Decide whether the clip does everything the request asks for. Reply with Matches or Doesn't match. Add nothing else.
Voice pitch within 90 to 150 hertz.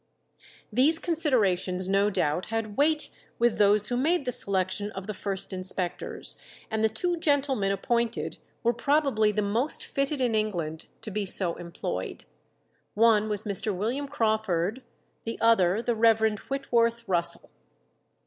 Doesn't match